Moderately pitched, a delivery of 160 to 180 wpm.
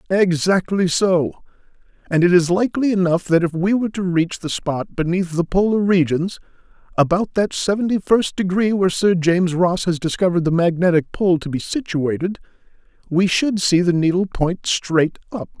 Yes: medium, 180 Hz; average, 170 wpm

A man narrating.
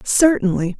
No: female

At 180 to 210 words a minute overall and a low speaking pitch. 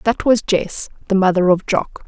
No: fast, 205 wpm; high, 200 Hz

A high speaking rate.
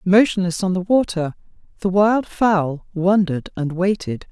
No: average, 140 wpm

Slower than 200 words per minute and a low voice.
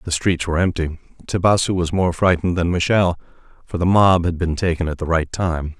No: fast, 205 wpm; very low, 85 Hz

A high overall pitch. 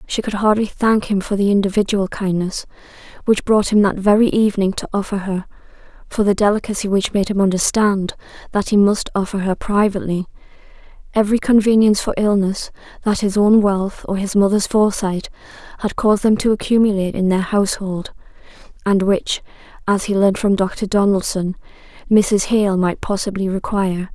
Yes: high, 200 Hz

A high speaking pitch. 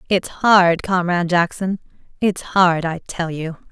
No: medium, 175 Hz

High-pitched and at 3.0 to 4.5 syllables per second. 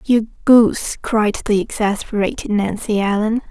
Yes: high, 215 Hz; 4.4 syllables/s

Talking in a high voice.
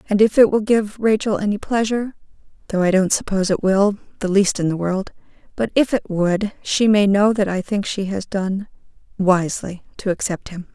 Yes: high, 200 Hz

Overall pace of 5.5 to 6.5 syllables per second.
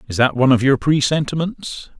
Yes: 5.7 syllables/s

